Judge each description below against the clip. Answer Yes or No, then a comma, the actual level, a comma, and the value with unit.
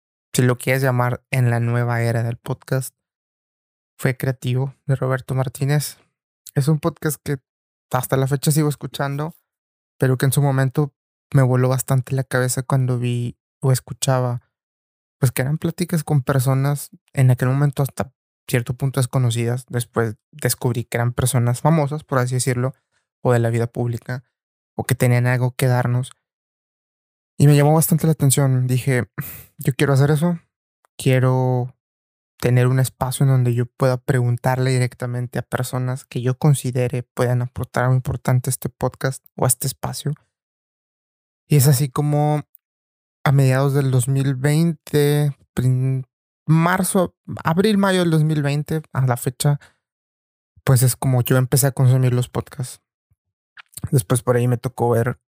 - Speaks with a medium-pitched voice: No, low, 130 Hz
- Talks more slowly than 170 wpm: Yes, average, 150 wpm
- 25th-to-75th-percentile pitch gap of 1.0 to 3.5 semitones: Yes, narrow, 2.6 semitones